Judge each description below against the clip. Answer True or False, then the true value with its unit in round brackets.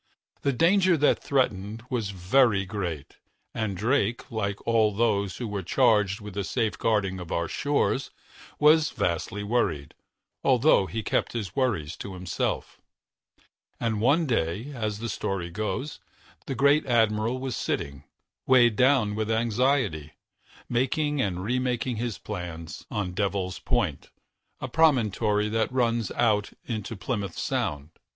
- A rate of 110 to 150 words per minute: True (135 wpm)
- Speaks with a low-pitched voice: True (110 Hz)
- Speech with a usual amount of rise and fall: True (4.4 semitones)